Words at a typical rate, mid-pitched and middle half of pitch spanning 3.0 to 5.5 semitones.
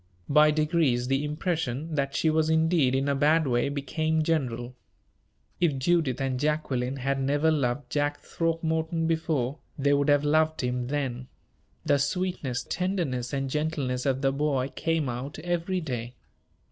Yes: average, 150 wpm; medium, 145 Hz; average, 3.4 semitones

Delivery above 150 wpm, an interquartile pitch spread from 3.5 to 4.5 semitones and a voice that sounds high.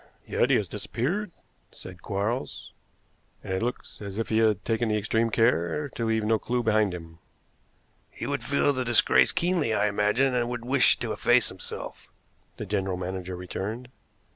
No: average, 165 wpm; average, 3.8 semitones; low, 110 Hz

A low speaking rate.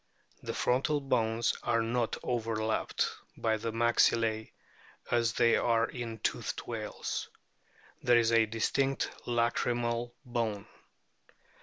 Yes: slow, 110 wpm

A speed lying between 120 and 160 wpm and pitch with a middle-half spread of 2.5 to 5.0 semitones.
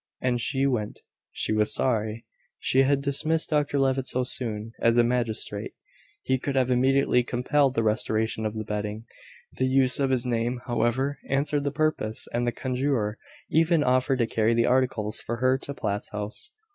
No: average, 175 wpm; average, 3.2 semitones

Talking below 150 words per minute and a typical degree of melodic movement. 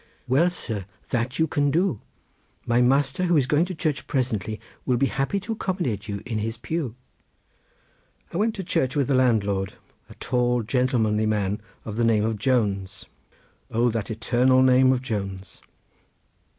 No: average, 165 wpm; average, 4.2 semitones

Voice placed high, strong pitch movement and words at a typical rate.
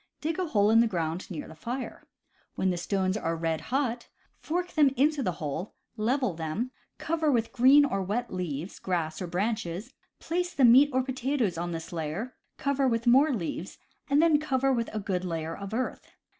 Yes: high, 225 Hz; wide, 7.4 semitones; average, 195 wpm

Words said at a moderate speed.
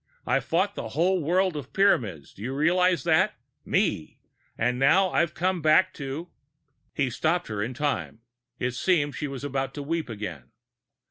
Yes: average, 175 wpm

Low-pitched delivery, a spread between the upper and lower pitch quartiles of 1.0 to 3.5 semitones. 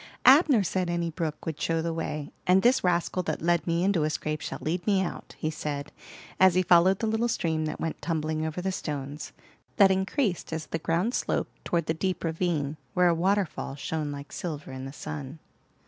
No: medium, 165 Hz; average, 3.2 semitones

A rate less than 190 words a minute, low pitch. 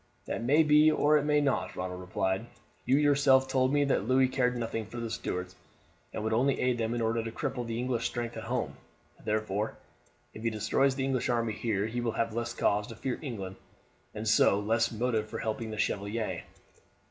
No: fast, 205 wpm; low, 115 Hz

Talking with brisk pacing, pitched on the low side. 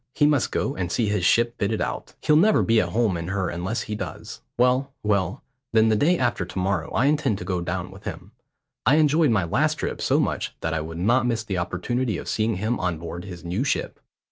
Yes: fast, 235 wpm; low, 105 Hz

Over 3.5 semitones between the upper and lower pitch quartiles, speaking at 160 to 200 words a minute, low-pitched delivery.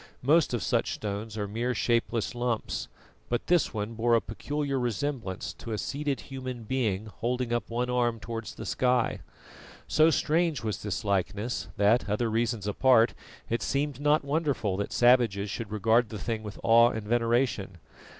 No: average, 3.0 semitones; average, 165 wpm; low, 115 Hz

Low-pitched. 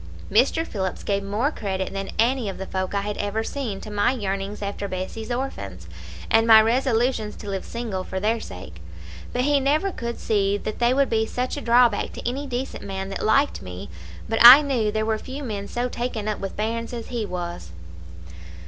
No: high, 220 Hz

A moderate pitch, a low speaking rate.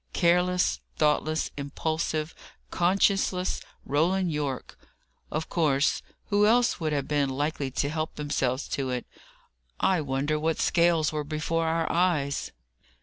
Yes: medium, 155 Hz; slow, 125 wpm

